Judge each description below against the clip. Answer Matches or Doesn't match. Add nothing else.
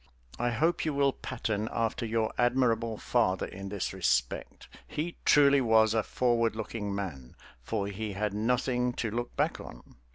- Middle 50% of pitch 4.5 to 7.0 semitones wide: Doesn't match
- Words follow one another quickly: Doesn't match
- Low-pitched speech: Matches